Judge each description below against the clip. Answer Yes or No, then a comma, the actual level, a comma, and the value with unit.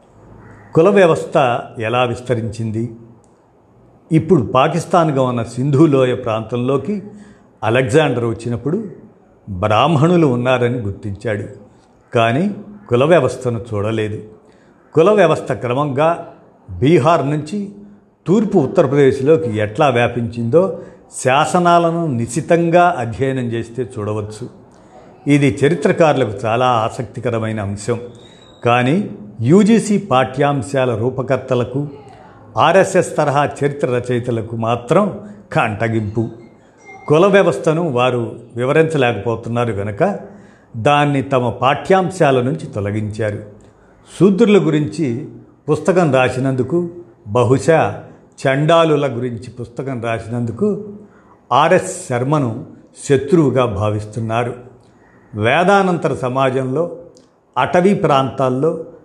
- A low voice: Yes, low, 130 Hz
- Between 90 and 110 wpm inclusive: No, average, 75 wpm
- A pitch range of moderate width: No, wide, 5.7 semitones